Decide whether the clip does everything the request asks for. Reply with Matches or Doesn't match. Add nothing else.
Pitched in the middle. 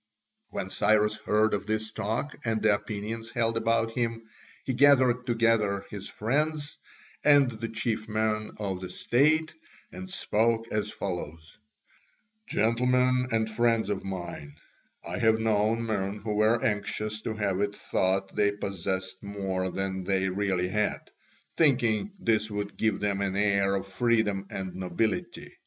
Doesn't match